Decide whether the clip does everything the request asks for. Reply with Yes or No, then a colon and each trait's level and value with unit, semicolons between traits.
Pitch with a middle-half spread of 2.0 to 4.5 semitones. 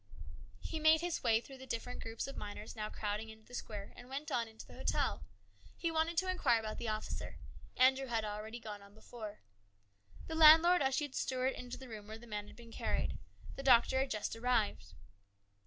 Yes: average, 3.8 semitones